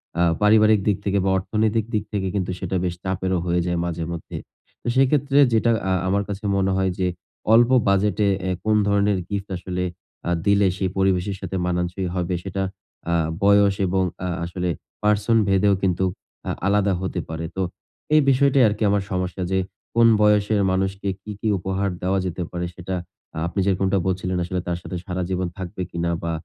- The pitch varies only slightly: Yes, narrow, 2.1 semitones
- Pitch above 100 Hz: No, very low, 95 Hz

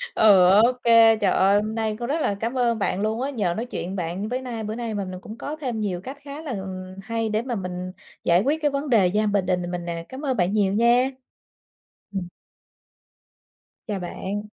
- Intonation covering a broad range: No, average, 4.3 semitones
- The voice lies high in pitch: Yes, high, 215 Hz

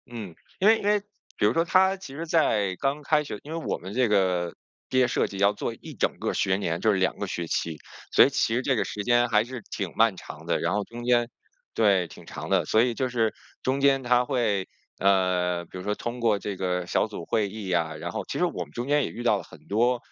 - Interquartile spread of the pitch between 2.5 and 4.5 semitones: No, average, 5.1 semitones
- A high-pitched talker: No, low, 110 Hz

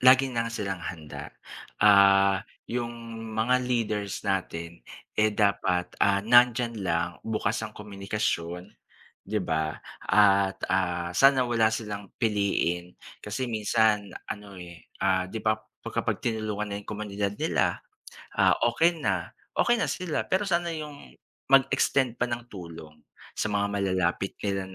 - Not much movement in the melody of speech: No, average, 3.6 semitones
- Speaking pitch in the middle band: No, low, 105 Hz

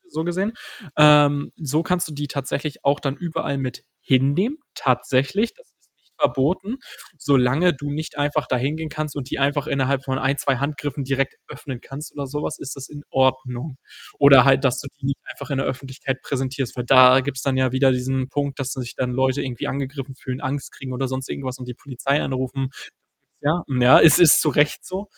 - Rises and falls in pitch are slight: Yes, narrow, 2.0 semitones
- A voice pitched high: No, low, 135 Hz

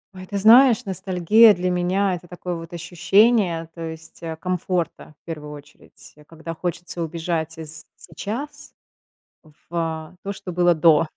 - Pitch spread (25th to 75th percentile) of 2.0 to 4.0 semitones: Yes, narrow, 2.6 semitones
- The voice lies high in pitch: No, medium, 175 Hz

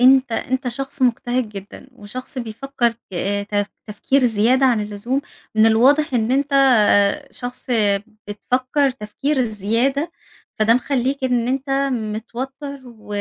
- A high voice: Yes, very high, 250 Hz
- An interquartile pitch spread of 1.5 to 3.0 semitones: No, average, 3.5 semitones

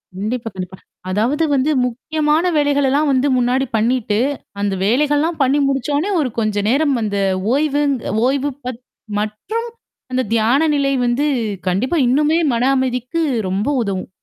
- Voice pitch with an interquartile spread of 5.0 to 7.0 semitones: No, average, 4.4 semitones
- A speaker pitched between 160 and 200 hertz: No, very high, 260 Hz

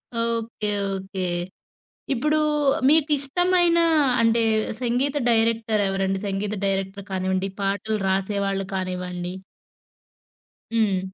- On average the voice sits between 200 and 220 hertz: Yes, high, 205 Hz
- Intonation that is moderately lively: Yes, average, 3.5 semitones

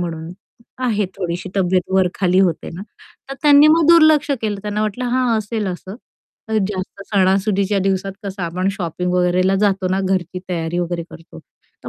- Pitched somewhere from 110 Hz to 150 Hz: No, high, 190 Hz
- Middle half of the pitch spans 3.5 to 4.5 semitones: No, average, 2.8 semitones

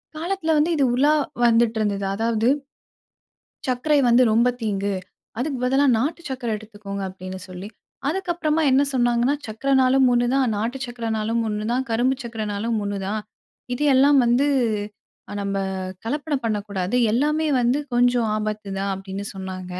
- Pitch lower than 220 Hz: No, high, 235 Hz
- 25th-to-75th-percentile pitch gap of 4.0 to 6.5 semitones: Yes, average, 4.3 semitones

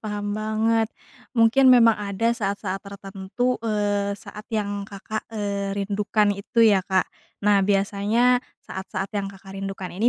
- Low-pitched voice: No, high, 205 Hz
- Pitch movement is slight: Yes, narrow, 1.9 semitones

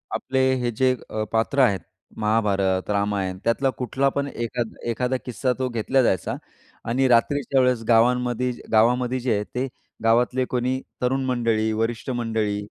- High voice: No, low, 120 Hz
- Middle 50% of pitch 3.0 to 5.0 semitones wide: No, narrow, 2.5 semitones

